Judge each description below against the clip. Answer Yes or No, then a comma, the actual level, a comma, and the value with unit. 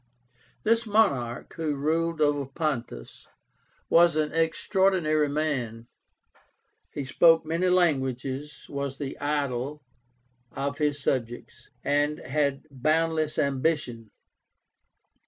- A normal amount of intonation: Yes, average, 3.1 semitones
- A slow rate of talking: Yes, slow, 95 wpm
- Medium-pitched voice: Yes, medium, 145 Hz